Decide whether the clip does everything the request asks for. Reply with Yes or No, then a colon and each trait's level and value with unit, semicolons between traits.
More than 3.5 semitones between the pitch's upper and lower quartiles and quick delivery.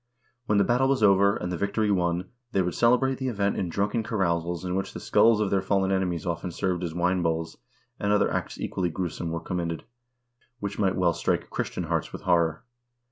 No: average, 2.8 semitones; fast, 210 wpm